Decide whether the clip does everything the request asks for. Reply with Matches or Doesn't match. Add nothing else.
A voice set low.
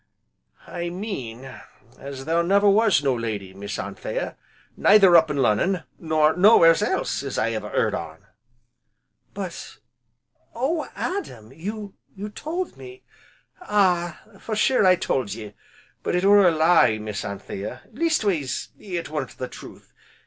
Doesn't match